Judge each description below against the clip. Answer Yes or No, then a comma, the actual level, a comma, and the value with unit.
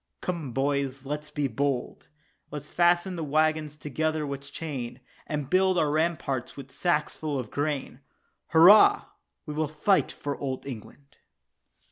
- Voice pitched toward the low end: No, medium, 150 Hz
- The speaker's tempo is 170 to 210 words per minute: No, average, 145 wpm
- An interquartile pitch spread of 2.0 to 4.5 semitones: Yes, narrow, 2.4 semitones